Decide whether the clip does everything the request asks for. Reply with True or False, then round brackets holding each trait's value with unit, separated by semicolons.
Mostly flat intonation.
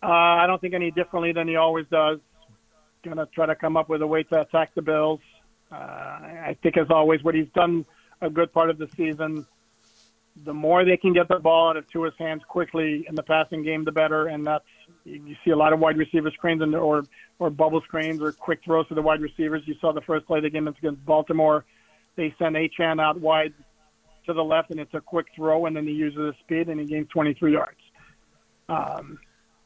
True (1.2 semitones)